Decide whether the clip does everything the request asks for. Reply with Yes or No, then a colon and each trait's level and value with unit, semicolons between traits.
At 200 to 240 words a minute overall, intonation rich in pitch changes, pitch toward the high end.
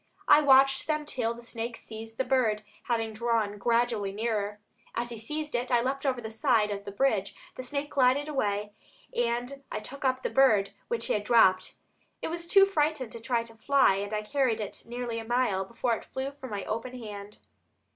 No: fast, 205 wpm; average, 3.7 semitones; high, 235 Hz